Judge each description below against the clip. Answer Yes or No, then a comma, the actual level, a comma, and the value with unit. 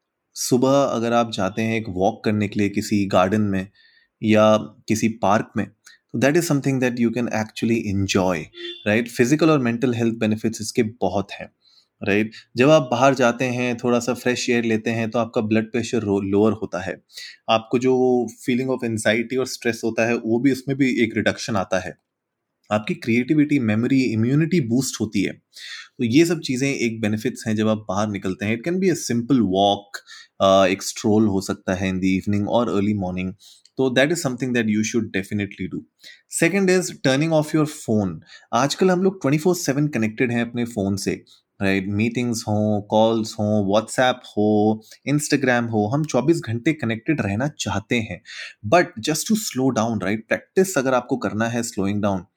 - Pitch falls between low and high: No, low, 115 Hz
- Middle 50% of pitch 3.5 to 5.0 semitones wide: Yes, average, 3.8 semitones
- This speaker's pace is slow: No, average, 185 wpm